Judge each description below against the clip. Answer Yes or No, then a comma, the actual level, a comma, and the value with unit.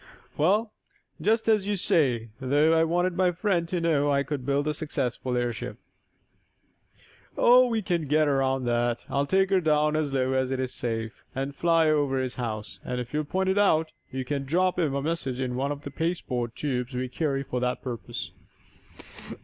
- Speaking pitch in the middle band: Yes, medium, 145 Hz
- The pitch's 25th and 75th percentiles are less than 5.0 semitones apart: Yes, average, 4.6 semitones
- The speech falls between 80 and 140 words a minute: No, average, 190 wpm